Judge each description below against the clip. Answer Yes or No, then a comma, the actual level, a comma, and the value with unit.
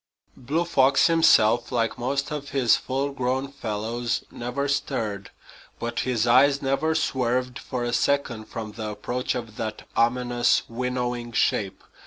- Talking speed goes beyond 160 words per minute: No, average, 140 wpm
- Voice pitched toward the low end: Yes, low, 125 Hz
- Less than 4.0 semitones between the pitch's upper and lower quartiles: Yes, average, 2.8 semitones